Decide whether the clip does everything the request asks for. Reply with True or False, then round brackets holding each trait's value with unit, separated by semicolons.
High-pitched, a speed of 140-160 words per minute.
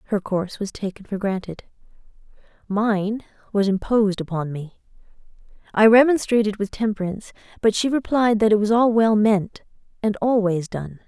True (210 Hz; 145 wpm)